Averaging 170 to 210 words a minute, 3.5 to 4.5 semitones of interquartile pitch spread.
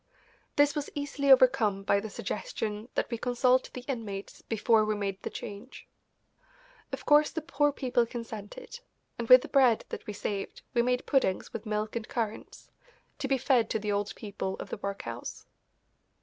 Yes: average, 175 wpm; average, 4.2 semitones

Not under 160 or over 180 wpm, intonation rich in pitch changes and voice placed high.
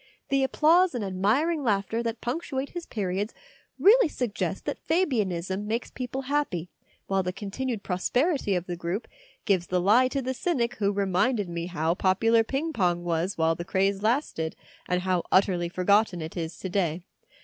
Yes: average, 170 wpm; wide, 6.2 semitones; high, 200 Hz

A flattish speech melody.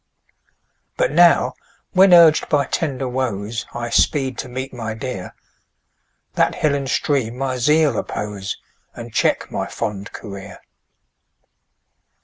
No: average, 4.2 semitones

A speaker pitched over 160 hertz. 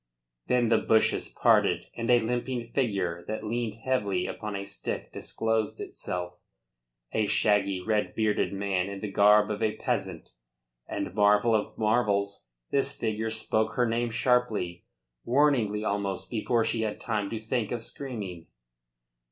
No: low, 110 Hz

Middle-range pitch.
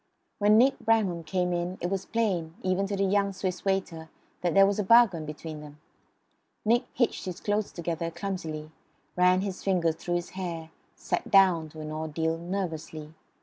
Yes: medium, 180 Hz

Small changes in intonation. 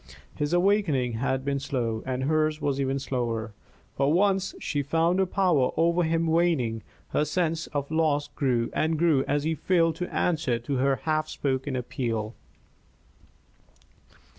No: average, 3.9 semitones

